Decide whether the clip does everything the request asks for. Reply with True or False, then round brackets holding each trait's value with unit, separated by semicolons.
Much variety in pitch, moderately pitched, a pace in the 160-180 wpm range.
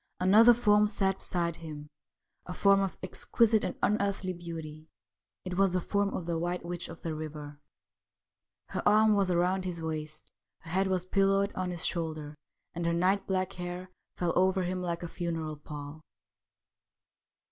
False (2.8 semitones; 180 Hz; 170 wpm)